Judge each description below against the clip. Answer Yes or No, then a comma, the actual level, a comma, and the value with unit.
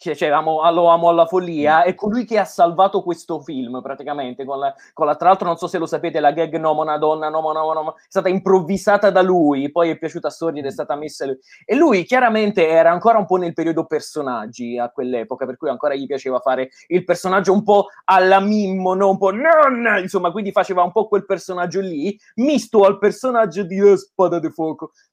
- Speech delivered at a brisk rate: Yes, fast, 220 wpm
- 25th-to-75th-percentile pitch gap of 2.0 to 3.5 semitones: No, average, 4.0 semitones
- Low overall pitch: No, medium, 175 Hz